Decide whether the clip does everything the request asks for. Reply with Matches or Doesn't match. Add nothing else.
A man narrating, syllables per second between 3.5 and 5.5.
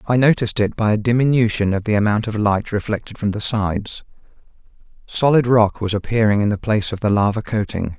Doesn't match